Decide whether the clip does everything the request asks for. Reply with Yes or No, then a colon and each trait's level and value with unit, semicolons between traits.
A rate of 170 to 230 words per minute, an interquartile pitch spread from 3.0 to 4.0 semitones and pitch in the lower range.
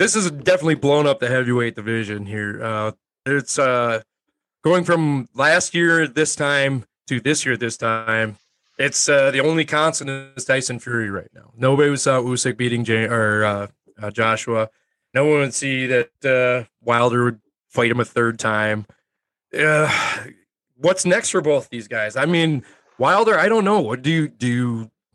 No: average, 175 wpm; average, 4.6 semitones; low, 125 Hz